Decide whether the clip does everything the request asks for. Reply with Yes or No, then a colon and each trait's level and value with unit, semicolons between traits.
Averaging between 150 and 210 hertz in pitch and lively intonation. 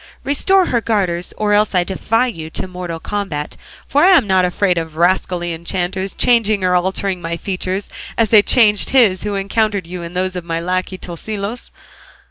No: high, 190 Hz; average, 3.1 semitones